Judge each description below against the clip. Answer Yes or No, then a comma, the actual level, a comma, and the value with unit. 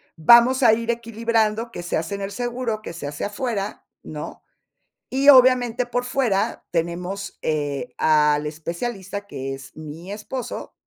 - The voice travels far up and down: Yes, wide, 6.3 semitones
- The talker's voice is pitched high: Yes, high, 205 Hz